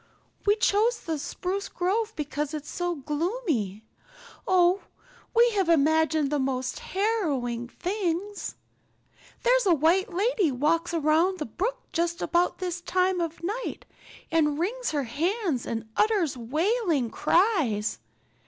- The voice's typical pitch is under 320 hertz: No, very high, 340 Hz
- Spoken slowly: Yes, slow, 130 wpm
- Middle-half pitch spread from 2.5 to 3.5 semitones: No, average, 5.2 semitones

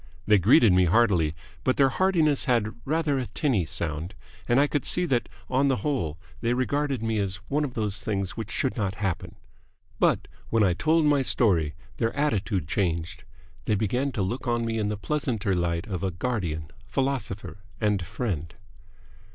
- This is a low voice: Yes, low, 110 Hz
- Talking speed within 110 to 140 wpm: No, average, 175 wpm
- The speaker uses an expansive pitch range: Yes, wide, 6.0 semitones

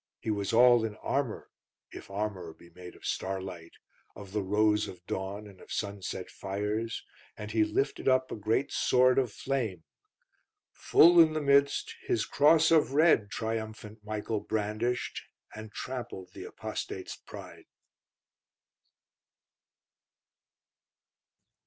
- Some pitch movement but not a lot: Yes, average, 4.0 semitones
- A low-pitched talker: Yes, low, 110 Hz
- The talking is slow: Yes, slow, 125 wpm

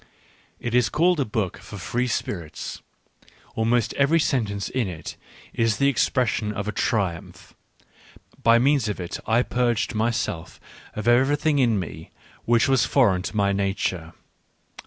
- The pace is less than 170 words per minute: Yes, average, 155 wpm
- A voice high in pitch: No, low, 115 Hz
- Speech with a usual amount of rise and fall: Yes, average, 4.0 semitones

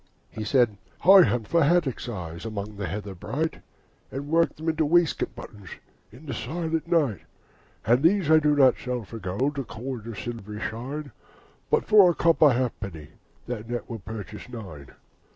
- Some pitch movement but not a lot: No, wide, 6.7 semitones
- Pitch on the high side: No, low, 125 Hz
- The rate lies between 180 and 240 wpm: No, average, 170 wpm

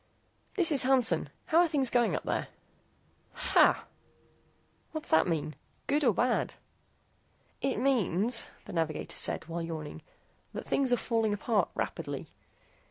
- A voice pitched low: No, high, 235 Hz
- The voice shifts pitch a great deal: Yes, wide, 7.8 semitones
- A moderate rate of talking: No, slow, 130 wpm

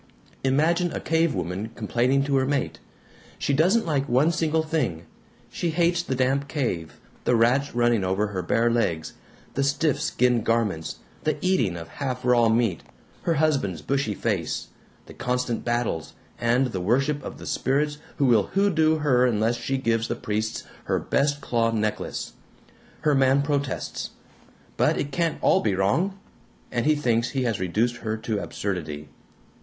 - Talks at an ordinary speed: Yes, average, 160 wpm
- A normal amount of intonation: Yes, average, 4.7 semitones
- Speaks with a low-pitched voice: Yes, low, 125 Hz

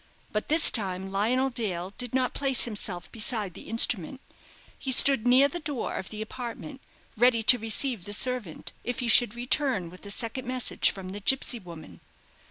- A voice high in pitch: Yes, high, 230 Hz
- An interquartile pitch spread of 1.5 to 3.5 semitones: No, average, 4.3 semitones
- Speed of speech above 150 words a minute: Yes, average, 180 wpm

